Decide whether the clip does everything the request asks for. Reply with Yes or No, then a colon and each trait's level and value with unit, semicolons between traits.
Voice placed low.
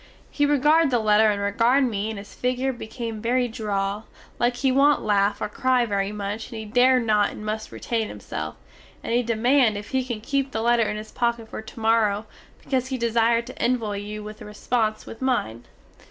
No: high, 225 Hz